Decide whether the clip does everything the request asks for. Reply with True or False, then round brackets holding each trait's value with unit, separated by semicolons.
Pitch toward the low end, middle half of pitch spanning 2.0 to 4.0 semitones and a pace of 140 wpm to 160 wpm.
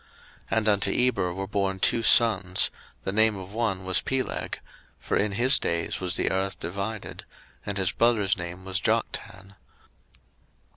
True (100 Hz; 2.7 semitones; 155 wpm)